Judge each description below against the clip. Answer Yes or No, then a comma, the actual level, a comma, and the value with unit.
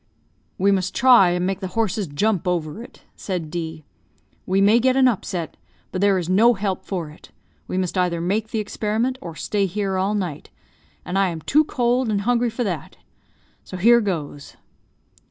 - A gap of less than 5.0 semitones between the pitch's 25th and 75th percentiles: Yes, average, 3.8 semitones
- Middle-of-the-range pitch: No, high, 195 Hz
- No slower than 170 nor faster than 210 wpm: Yes, average, 185 wpm